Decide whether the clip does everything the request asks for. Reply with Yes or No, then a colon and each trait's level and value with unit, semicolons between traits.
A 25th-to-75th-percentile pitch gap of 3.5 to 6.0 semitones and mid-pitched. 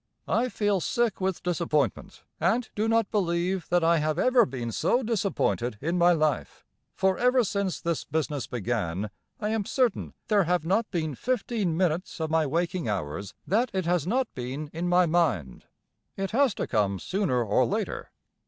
Yes: wide, 5.6 semitones; medium, 175 Hz